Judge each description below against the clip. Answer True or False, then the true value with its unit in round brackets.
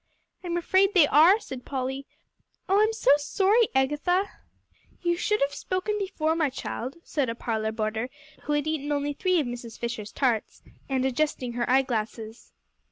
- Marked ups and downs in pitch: True (6.3 semitones)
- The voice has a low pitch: False (285 Hz)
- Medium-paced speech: True (165 wpm)